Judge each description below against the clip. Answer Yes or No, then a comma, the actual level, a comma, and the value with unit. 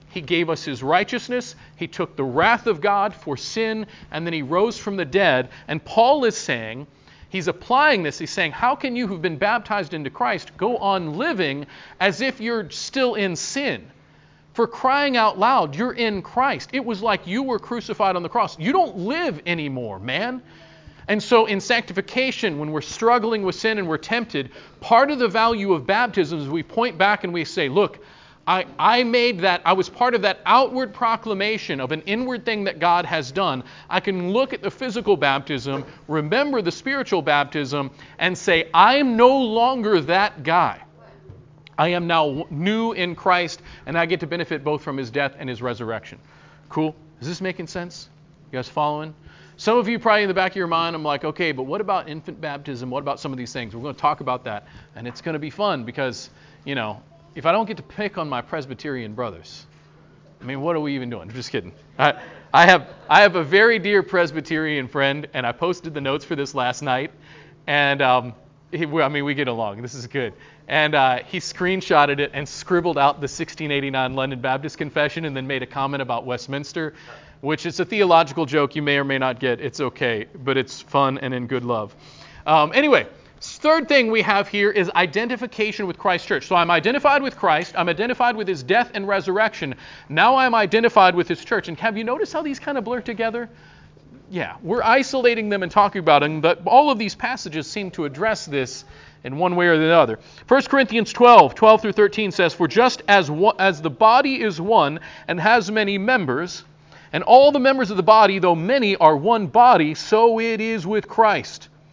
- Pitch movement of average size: No, wide, 7.0 semitones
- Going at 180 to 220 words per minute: Yes, fast, 205 wpm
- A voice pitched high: No, medium, 175 Hz